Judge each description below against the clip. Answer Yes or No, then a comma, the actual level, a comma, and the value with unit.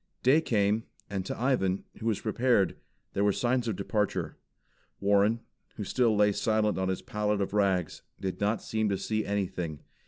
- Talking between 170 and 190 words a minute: Yes, average, 175 wpm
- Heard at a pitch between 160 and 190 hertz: No, low, 105 Hz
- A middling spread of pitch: No, narrow, 2.3 semitones